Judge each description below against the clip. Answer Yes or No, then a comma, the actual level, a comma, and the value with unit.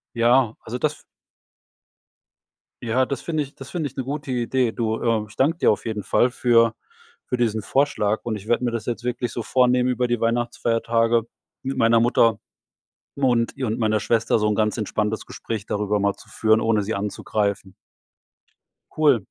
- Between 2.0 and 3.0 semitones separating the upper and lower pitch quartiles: Yes, narrow, 2.4 semitones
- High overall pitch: No, low, 115 Hz